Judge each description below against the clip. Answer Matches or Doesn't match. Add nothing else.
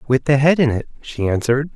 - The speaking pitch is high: Doesn't match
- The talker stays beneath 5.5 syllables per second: Doesn't match